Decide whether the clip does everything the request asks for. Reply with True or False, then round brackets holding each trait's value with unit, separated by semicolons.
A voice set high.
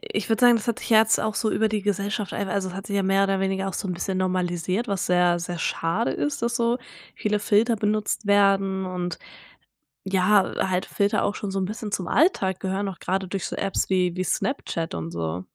True (195 Hz)